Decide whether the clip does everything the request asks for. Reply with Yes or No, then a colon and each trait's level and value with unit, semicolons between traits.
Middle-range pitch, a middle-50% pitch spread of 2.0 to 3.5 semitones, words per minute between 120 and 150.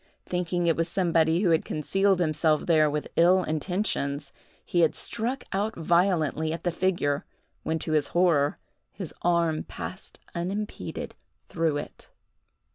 Yes: medium, 170 Hz; average, 2.8 semitones; average, 140 wpm